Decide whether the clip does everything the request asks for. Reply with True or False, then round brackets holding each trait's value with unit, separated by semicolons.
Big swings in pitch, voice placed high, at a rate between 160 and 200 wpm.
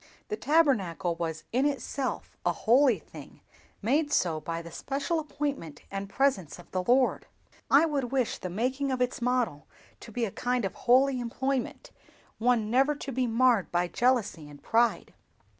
True (5.9 semitones; 245 Hz; 165 wpm)